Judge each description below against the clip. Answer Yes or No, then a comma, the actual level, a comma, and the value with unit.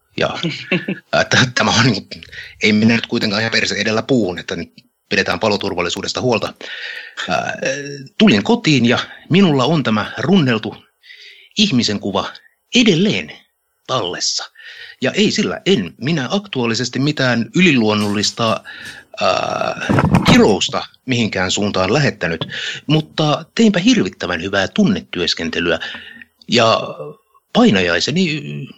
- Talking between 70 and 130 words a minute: Yes, average, 100 wpm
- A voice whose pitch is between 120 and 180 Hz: Yes, medium, 140 Hz